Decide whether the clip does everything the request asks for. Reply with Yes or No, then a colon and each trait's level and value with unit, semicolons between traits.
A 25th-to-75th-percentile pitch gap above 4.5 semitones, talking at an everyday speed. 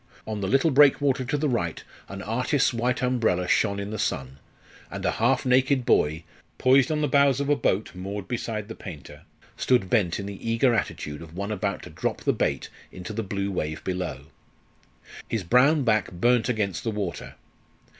Yes: average, 5.1 semitones; average, 185 wpm